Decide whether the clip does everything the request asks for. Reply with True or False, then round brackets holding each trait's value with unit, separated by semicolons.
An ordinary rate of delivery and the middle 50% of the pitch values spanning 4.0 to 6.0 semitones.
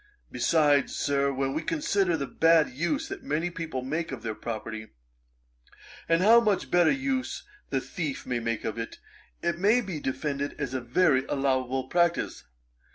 True (160 wpm; 4.8 semitones)